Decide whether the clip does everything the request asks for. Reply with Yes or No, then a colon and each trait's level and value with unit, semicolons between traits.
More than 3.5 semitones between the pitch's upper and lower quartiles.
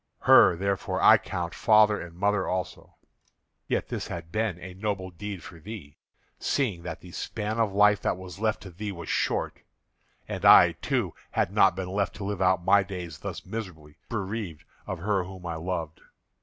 No: average, 3.1 semitones